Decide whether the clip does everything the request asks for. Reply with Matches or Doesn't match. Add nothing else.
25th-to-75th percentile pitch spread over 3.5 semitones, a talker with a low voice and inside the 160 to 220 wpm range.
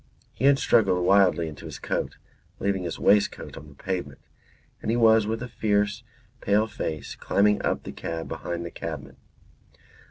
Matches